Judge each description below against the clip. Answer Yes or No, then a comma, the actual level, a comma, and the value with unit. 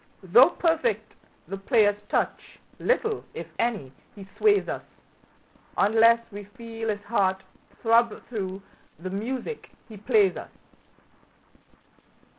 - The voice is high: Yes, high, 225 Hz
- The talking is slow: Yes, slow, 110 wpm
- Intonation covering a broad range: No, average, 3.4 semitones